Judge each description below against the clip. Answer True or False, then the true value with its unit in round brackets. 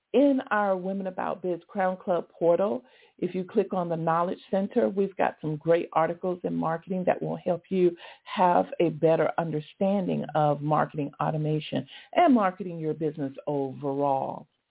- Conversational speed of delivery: True (155 wpm)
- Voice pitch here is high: False (175 Hz)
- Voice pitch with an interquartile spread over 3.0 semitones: True (3.8 semitones)